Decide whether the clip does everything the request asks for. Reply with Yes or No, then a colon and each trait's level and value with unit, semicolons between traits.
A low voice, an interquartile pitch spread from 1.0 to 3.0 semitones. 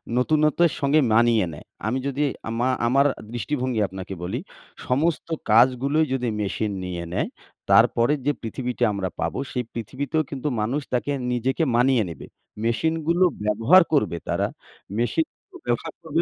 No: low, 125 Hz; average, 4.7 semitones